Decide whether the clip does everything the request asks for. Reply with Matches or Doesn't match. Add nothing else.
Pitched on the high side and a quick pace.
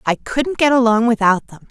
Matches